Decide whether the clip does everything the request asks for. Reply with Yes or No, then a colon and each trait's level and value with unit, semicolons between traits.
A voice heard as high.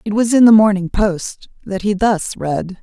Yes: high, 200 Hz